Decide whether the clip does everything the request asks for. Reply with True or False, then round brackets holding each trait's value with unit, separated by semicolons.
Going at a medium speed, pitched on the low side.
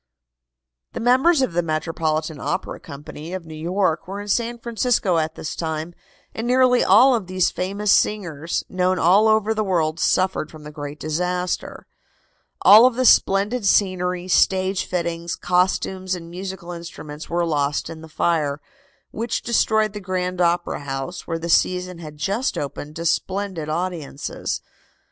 False (155 wpm; 180 Hz)